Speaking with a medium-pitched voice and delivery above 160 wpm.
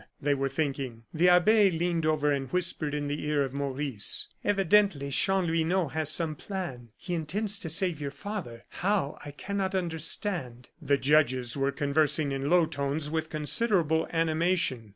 No: medium, 155 Hz; average, 155 wpm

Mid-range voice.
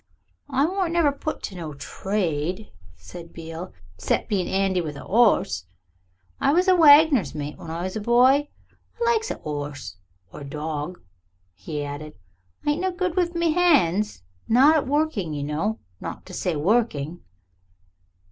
No: high, 195 Hz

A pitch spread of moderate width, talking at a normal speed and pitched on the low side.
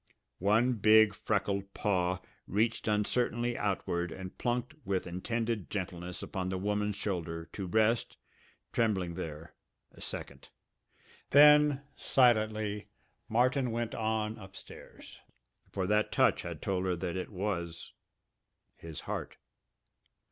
No: average, 3.6 semitones; slow, 115 wpm; low, 105 Hz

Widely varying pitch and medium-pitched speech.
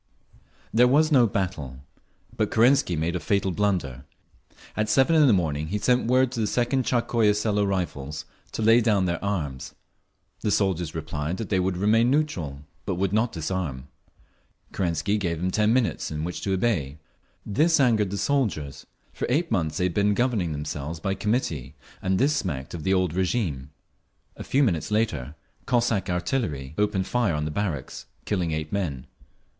No: wide, 6.2 semitones; very low, 95 Hz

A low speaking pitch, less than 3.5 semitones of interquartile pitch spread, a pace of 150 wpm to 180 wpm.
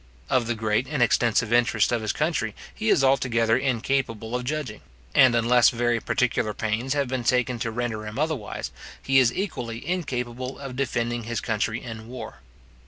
Yes: low, 120 Hz; narrow, 2.4 semitones; average, 170 wpm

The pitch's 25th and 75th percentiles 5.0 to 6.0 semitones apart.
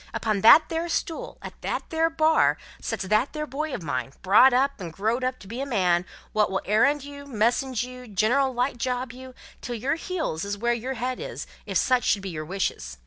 Yes: average, 5.3 semitones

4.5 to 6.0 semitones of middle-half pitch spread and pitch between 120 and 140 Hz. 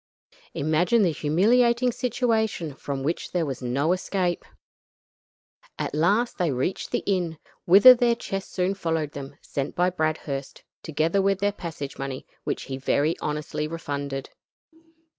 No: wide, 5.4 semitones; medium, 165 Hz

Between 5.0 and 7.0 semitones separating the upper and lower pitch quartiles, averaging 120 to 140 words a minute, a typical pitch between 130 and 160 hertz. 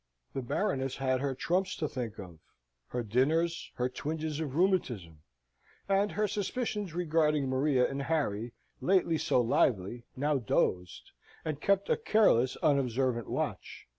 Yes: wide, 5.4 semitones; slow, 135 wpm; medium, 140 Hz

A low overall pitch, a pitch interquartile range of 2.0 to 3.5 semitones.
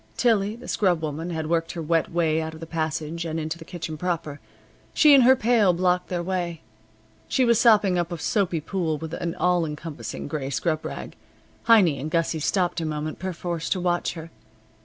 No: medium, 170 Hz; narrow, 2.6 semitones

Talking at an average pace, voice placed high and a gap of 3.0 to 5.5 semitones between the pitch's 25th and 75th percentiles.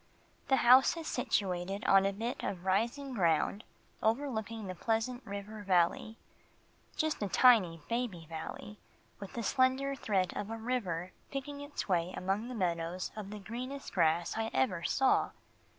Yes: average, 150 wpm; high, 210 Hz; average, 5.2 semitones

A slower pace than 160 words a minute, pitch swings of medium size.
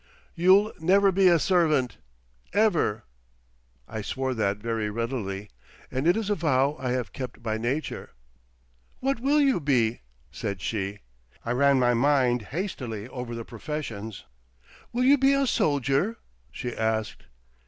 No: average, 140 wpm; wide, 7.8 semitones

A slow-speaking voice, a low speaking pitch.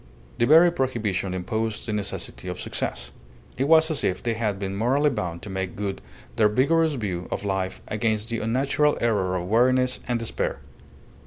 No: average, 175 wpm; low, 110 Hz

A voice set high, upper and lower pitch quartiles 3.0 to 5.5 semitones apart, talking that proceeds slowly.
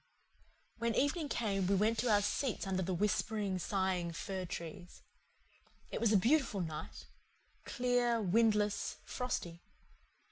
Yes: high, 205 Hz; average, 3.9 semitones; slow, 130 wpm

